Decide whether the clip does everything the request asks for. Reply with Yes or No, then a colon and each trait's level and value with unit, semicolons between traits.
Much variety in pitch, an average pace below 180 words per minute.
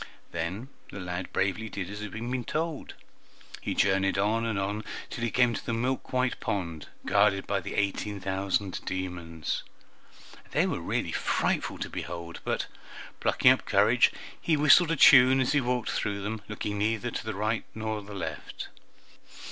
No: average, 3.8 semitones; average, 170 wpm